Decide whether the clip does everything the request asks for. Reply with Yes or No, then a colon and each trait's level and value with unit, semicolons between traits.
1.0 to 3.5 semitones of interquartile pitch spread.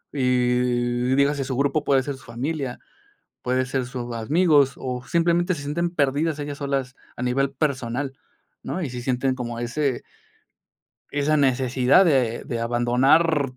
Yes: average, 2.7 semitones